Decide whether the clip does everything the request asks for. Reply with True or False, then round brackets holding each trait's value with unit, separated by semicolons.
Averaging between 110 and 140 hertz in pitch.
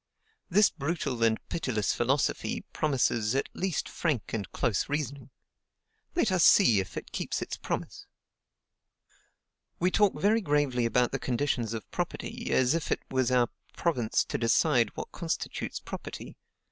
True (135 Hz)